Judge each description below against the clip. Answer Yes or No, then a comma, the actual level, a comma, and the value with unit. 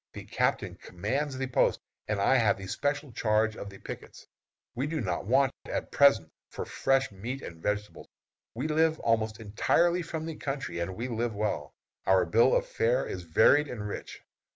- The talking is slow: No, average, 180 wpm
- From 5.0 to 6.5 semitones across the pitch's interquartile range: Yes, average, 5.3 semitones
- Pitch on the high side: No, low, 115 Hz